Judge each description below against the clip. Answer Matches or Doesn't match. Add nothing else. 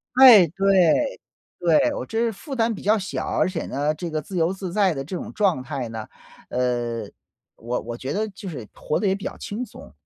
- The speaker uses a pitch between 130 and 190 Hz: Matches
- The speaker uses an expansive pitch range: Matches